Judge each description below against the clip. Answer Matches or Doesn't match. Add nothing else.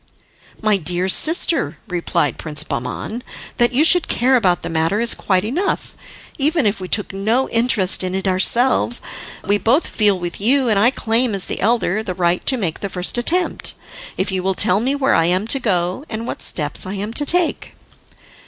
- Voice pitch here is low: Doesn't match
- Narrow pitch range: Doesn't match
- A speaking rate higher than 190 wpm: Matches